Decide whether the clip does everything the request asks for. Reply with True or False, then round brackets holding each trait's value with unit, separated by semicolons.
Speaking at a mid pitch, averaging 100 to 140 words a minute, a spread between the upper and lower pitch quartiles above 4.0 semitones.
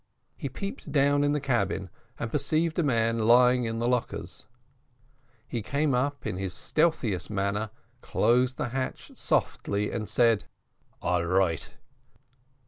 False (120 Hz; 135 wpm; 5.2 semitones)